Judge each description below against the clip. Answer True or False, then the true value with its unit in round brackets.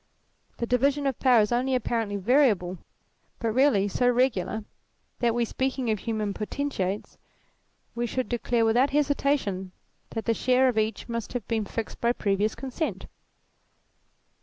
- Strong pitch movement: False (3.4 semitones)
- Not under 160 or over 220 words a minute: False (150 wpm)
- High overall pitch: True (235 Hz)